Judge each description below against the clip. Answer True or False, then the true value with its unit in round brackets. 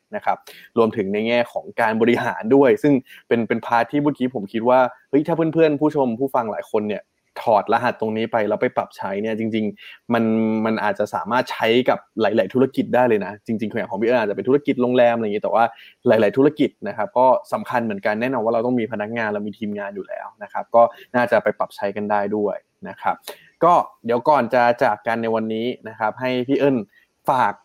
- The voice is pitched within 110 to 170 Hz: True (115 Hz)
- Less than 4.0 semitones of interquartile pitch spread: True (2.5 semitones)